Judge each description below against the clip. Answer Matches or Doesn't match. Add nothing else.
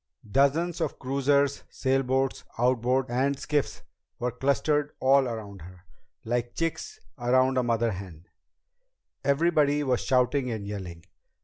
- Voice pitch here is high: Doesn't match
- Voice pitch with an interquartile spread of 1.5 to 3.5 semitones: Matches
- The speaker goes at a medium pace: Doesn't match